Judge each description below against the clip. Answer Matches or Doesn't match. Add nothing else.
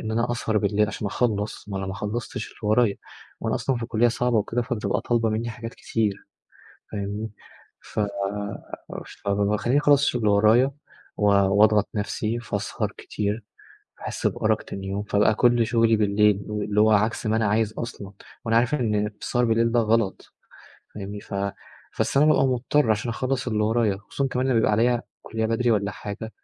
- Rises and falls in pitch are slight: Matches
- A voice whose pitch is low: Matches